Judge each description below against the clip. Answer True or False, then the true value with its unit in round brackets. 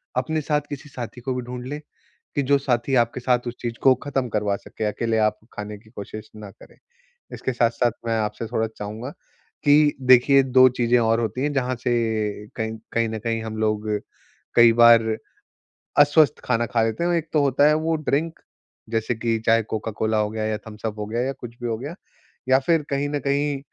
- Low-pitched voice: True (120 Hz)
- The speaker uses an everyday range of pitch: True (3.7 semitones)